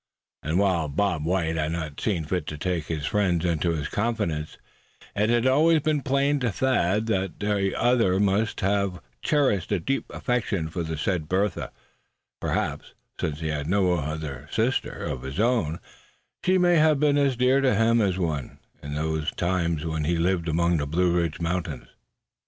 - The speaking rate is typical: Yes, average, 175 wpm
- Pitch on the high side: No, very low, 90 Hz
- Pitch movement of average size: No, wide, 6.1 semitones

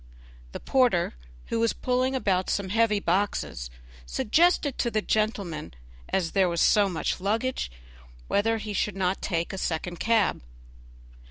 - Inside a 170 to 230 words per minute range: No, average, 145 wpm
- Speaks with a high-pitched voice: Yes, high, 205 Hz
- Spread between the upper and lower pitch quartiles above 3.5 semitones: Yes, average, 4.1 semitones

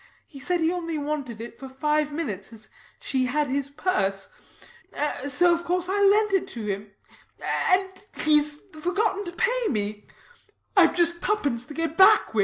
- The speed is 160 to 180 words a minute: Yes, average, 170 wpm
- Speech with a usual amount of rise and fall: No, wide, 5.9 semitones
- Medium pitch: No, very high, 305 Hz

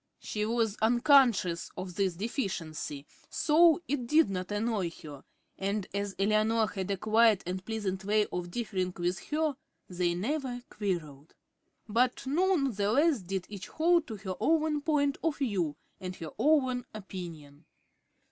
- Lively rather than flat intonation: Yes, wide, 6.1 semitones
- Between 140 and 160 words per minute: Yes, average, 145 wpm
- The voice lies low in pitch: No, high, 210 Hz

